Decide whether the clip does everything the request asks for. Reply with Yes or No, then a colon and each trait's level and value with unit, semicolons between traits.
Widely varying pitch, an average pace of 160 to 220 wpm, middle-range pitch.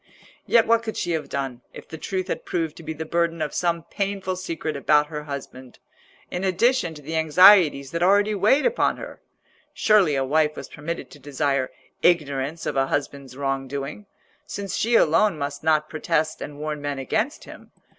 No: average, 4.6 semitones; average, 185 wpm; medium, 155 Hz